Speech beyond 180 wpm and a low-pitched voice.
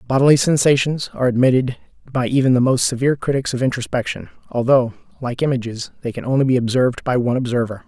No: average, 175 wpm; low, 125 Hz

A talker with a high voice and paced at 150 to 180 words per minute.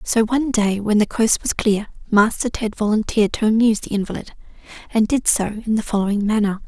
No: high, 215 Hz; average, 200 wpm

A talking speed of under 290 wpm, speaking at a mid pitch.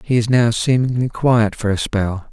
No: fast, 205 wpm; low, 115 Hz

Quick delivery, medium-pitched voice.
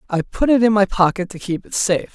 No: fast, 280 wpm; high, 195 Hz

